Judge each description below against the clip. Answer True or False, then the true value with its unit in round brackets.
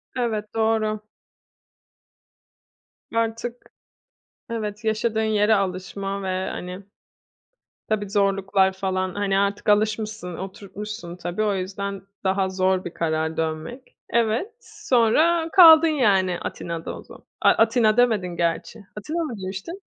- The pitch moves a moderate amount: True (3.1 semitones)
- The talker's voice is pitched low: False (205 Hz)